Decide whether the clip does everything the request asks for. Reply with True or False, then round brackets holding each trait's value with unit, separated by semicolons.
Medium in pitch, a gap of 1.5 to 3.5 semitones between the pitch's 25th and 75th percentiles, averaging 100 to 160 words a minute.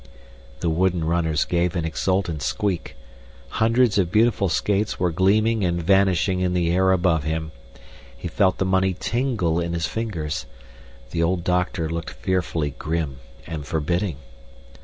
False (90 Hz; 2.8 semitones; 145 wpm)